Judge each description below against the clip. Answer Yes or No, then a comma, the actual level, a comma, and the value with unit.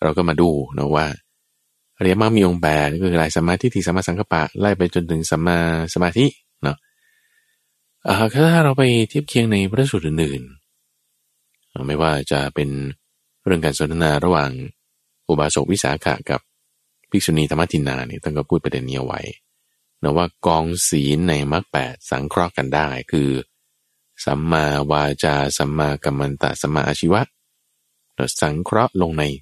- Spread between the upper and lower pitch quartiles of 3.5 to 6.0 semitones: Yes, average, 4.2 semitones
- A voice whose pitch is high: No, very low, 80 Hz